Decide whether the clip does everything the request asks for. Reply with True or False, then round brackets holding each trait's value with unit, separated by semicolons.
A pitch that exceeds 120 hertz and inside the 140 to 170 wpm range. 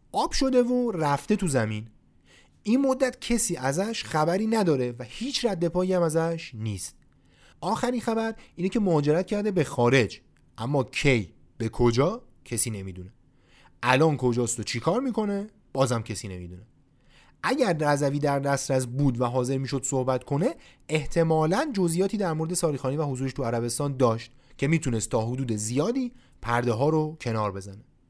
True (140 Hz; 150 wpm)